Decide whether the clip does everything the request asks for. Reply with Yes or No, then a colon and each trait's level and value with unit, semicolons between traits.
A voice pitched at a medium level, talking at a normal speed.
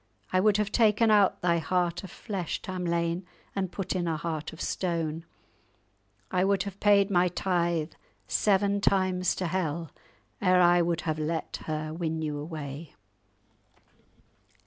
Yes: medium, 175 Hz; average, 145 wpm